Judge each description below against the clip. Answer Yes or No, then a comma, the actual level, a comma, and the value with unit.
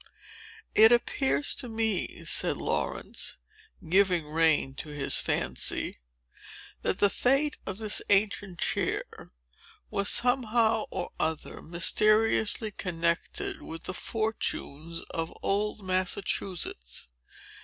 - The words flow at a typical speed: No, slow, 105 wpm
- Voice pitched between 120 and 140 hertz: No, high, 195 Hz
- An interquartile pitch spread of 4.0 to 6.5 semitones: Yes, average, 4.9 semitones